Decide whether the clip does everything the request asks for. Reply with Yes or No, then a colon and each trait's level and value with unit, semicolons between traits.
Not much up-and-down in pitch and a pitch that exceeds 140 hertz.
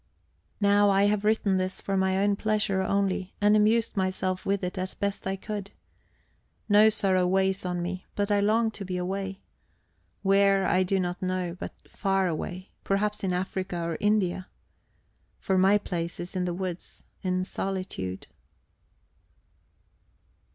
Yes: narrow, 1.6 semitones; high, 190 Hz